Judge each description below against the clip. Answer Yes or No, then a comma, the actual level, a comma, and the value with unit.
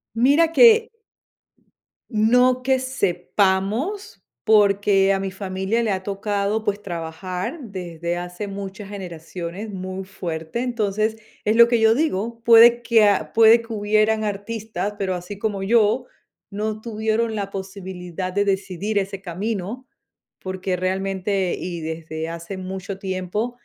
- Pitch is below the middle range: No, high, 200 Hz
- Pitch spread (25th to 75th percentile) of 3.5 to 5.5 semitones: No, average, 2.9 semitones